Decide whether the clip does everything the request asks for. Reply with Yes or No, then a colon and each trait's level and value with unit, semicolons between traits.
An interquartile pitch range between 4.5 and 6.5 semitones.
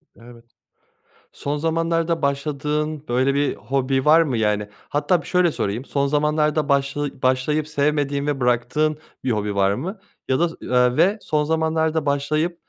No: average, 3.0 semitones